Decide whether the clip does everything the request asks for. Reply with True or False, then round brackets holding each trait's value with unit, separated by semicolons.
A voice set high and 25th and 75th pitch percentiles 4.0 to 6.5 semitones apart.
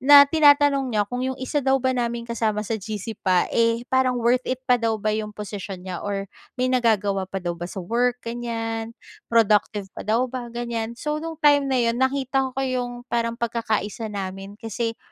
False (235 Hz; 3.3 semitones)